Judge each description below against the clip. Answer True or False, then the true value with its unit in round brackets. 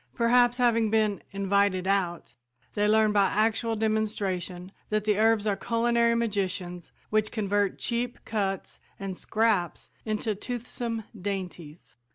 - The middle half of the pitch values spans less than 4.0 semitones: True (2.7 semitones)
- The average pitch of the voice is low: False (210 Hz)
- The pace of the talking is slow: True (125 wpm)